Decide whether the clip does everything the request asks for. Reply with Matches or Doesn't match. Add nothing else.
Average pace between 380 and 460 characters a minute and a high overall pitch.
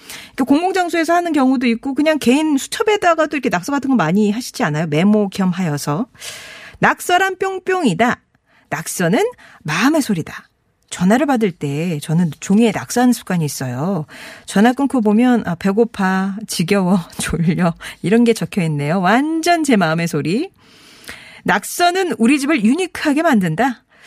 Doesn't match